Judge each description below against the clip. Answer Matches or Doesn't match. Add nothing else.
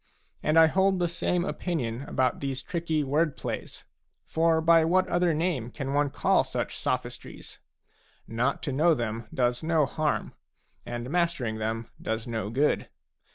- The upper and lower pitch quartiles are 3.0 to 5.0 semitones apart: Doesn't match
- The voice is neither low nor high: Matches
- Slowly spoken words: Doesn't match